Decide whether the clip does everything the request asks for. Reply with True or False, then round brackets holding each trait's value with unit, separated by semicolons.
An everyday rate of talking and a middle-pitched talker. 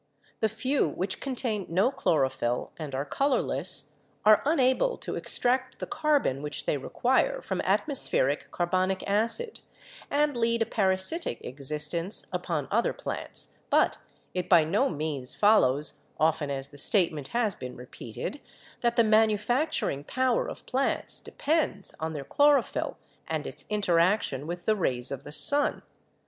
False (145 wpm; 195 Hz)